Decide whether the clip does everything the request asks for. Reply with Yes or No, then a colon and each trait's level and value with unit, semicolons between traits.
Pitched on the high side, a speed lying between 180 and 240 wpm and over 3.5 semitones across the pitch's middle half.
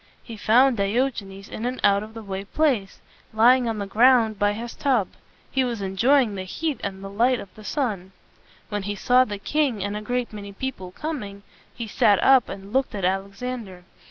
Yes: high, 215 Hz; fast, 205 wpm; average, 4.1 semitones